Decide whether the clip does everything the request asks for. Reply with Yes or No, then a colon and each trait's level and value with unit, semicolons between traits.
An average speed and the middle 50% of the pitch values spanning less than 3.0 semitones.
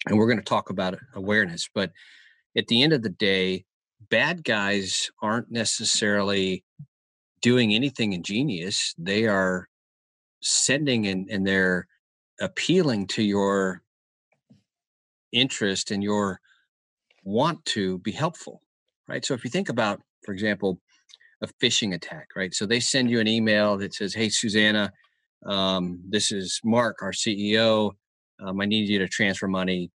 Yes: average, 145 wpm; narrow, 2.6 semitones